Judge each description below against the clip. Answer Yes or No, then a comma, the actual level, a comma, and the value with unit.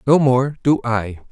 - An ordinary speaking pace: Yes, average, 180 wpm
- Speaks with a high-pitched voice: No, low, 125 Hz